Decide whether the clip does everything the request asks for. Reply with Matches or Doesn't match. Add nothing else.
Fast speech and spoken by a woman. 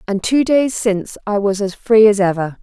Matches